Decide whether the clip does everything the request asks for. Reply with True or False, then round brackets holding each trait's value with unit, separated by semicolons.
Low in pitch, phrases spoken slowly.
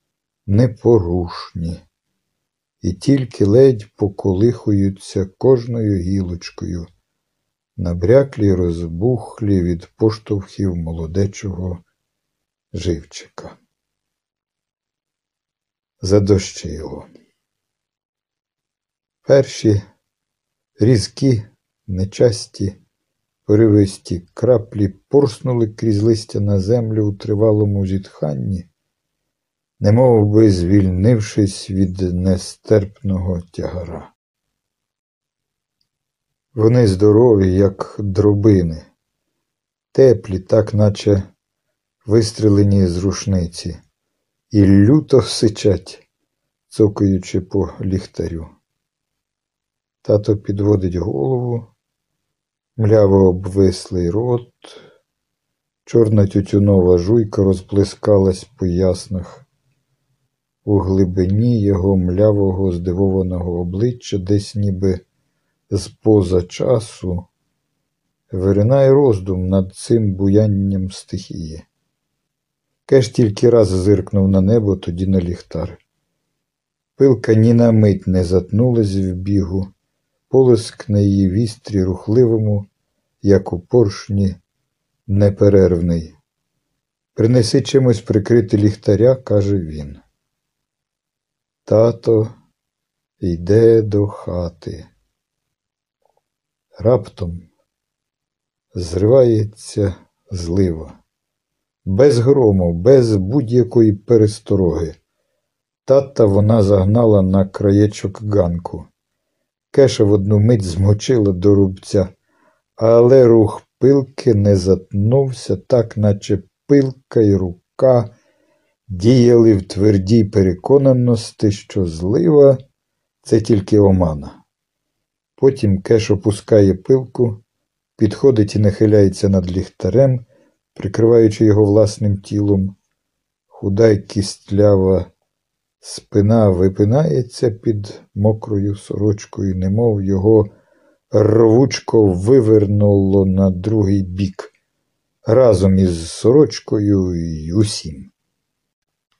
True (105 Hz; 75 wpm)